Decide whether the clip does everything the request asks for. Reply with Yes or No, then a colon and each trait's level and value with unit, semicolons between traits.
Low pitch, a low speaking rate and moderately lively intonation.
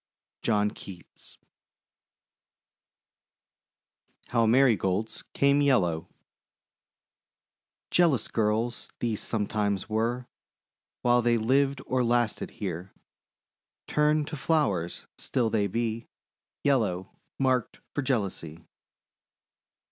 Yes: low, 115 Hz; slow, 80 wpm; average, 4.1 semitones